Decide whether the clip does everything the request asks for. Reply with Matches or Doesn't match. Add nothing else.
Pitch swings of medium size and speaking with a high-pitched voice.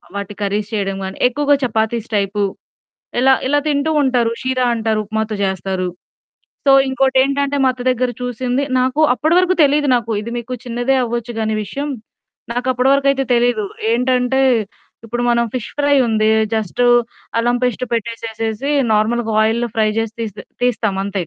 Matches